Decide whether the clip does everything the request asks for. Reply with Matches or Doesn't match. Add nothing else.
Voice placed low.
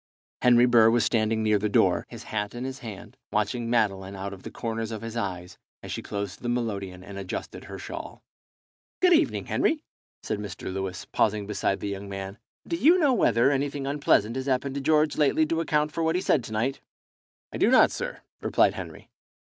Matches